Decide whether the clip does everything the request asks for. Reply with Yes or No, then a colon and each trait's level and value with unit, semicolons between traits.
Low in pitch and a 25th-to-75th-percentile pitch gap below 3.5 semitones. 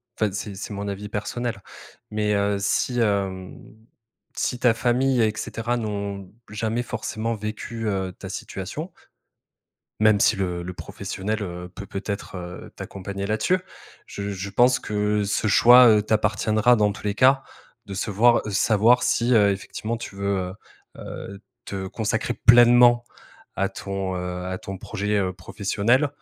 Yes: low, 105 Hz; average, 2.8 semitones